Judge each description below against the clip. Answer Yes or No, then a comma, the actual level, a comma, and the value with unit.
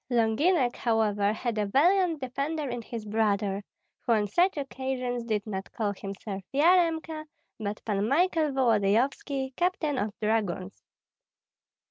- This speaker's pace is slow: Yes, slow, 125 wpm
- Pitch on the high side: Yes, high, 240 Hz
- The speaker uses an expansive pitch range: Yes, wide, 5.8 semitones